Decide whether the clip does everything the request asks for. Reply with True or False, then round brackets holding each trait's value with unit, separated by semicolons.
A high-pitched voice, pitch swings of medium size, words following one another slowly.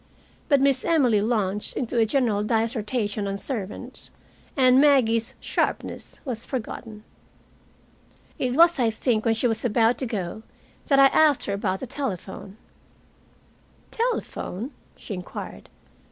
True (230 Hz; 3.9 semitones; 130 wpm)